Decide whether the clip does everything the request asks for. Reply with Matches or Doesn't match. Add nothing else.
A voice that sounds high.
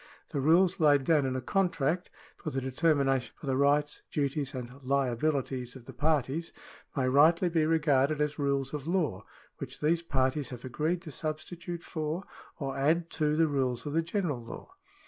Doesn't match